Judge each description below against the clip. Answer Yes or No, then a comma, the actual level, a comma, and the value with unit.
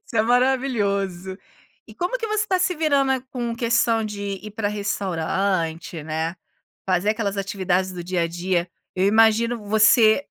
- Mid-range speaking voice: No, high, 205 Hz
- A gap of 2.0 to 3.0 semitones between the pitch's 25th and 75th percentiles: No, average, 4.2 semitones